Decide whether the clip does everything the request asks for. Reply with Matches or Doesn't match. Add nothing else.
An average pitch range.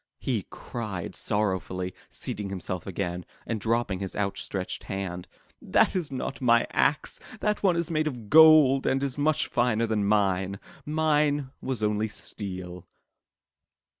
Doesn't match